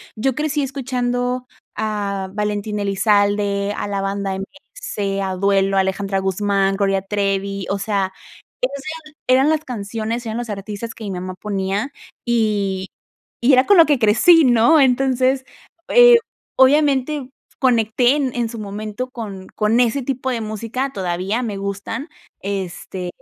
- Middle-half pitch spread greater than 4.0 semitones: Yes, average, 4.6 semitones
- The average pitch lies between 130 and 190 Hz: No, high, 215 Hz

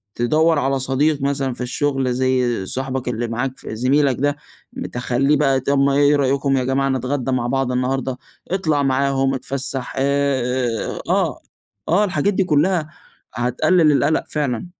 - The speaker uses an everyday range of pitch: No, narrow, 2.1 semitones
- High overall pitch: No, low, 135 Hz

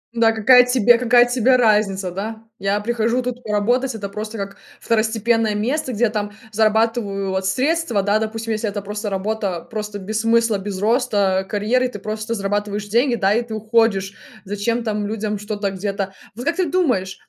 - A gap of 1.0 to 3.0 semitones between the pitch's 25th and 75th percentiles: Yes, narrow, 2.5 semitones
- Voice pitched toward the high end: Yes, high, 215 Hz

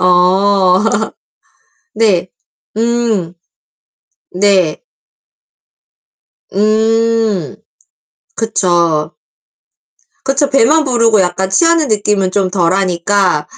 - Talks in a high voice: Yes, high, 200 Hz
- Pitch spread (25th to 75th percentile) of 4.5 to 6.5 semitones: No, average, 3.8 semitones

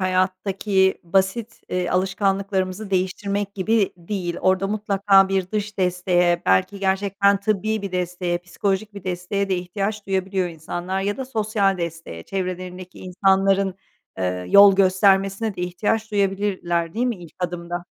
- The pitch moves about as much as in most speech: No, narrow, 1.9 semitones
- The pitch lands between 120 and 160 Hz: No, high, 190 Hz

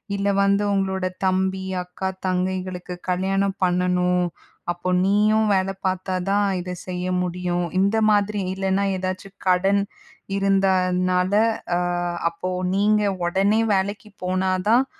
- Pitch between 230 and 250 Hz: No, high, 190 Hz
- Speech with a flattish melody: Yes, narrow, 1.5 semitones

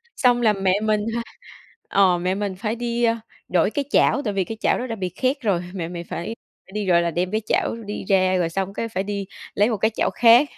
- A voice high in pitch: Yes, high, 205 Hz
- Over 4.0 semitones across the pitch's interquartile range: No, average, 3.7 semitones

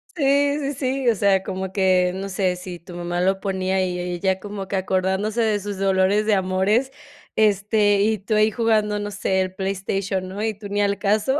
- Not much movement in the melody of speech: Yes, narrow, 2.1 semitones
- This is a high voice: Yes, high, 195 Hz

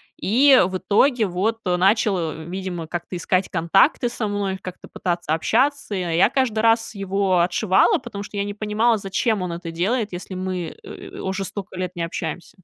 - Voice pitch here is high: Yes, high, 195 Hz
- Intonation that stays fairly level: No, average, 3.3 semitones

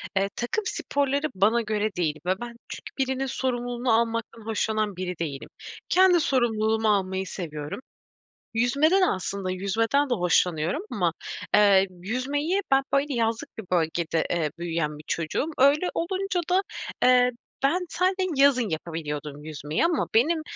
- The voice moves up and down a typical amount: No, wide, 7.4 semitones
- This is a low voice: No, high, 225 Hz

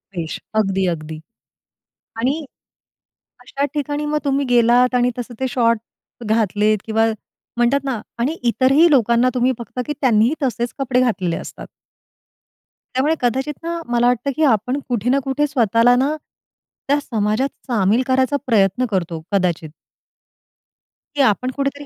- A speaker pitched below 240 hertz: No, high, 245 Hz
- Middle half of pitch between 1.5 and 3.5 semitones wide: No, average, 4.0 semitones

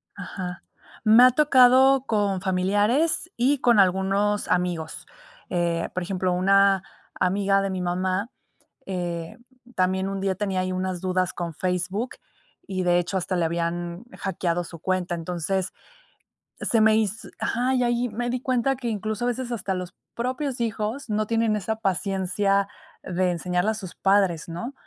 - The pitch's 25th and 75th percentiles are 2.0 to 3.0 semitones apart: No, average, 3.7 semitones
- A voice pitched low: No, high, 195 Hz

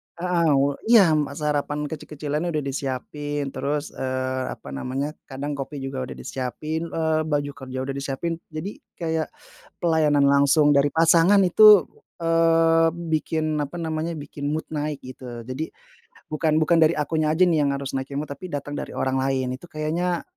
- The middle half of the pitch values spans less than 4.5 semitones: Yes, average, 2.7 semitones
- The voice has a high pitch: No, medium, 150 Hz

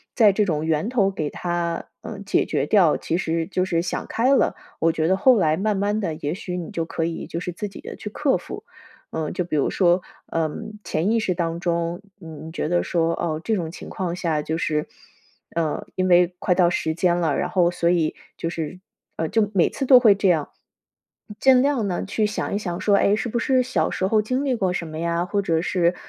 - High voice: No, medium, 175 Hz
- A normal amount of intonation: Yes, average, 3.7 semitones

